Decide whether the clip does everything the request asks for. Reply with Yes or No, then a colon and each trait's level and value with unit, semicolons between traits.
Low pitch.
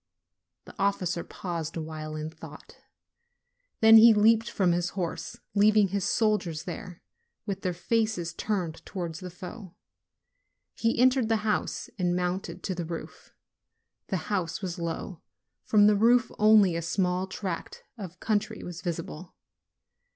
No: medium, 185 Hz